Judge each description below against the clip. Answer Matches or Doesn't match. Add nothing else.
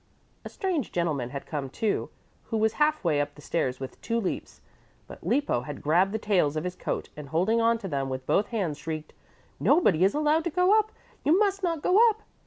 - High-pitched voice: Matches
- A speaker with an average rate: Doesn't match